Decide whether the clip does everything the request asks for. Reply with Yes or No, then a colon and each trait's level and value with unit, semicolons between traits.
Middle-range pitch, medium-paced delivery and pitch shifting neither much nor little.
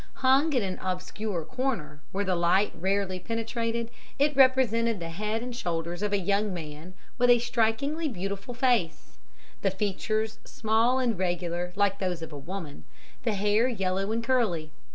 No: high, 205 Hz; average, 160 wpm; average, 4.5 semitones